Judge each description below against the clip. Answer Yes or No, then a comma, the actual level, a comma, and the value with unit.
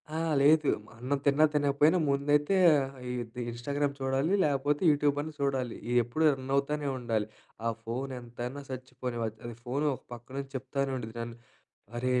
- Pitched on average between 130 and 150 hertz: Yes, low, 135 Hz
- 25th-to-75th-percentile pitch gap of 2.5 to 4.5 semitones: Yes, average, 2.8 semitones